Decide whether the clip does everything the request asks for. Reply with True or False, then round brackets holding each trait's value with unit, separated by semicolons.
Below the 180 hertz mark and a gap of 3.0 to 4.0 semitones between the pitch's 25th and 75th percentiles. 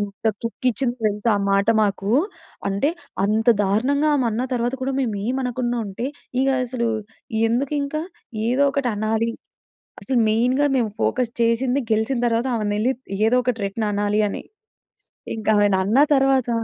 False (235 Hz; 3.3 semitones)